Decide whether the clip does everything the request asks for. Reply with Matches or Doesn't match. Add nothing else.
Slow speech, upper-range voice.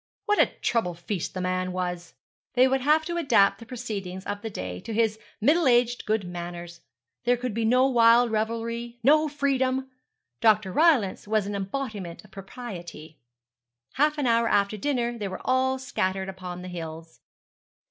Doesn't match